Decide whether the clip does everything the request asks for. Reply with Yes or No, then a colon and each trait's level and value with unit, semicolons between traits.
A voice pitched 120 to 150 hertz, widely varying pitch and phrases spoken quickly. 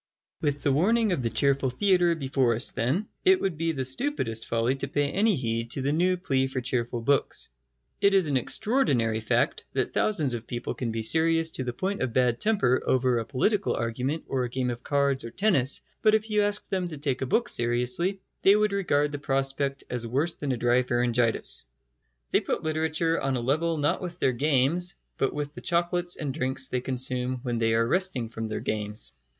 Yes: low, 135 Hz; wide, 5.7 semitones; fast, 210 wpm